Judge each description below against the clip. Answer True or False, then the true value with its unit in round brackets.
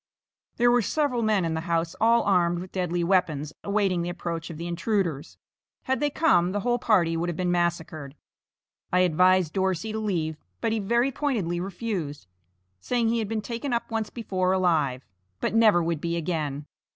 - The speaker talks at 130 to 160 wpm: False (185 wpm)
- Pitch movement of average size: True (4.7 semitones)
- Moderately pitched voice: True (180 Hz)